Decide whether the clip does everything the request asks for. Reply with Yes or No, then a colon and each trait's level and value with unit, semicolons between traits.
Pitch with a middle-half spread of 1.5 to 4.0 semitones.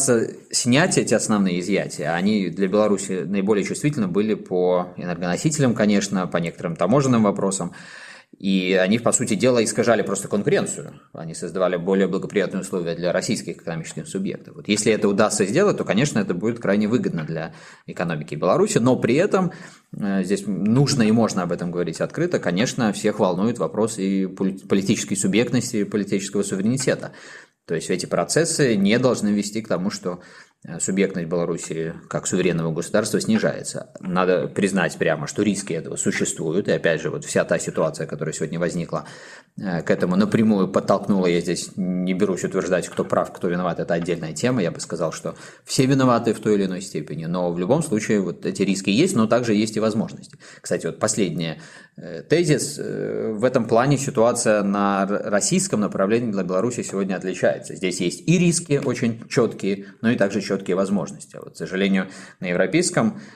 No: average, 4.7 semitones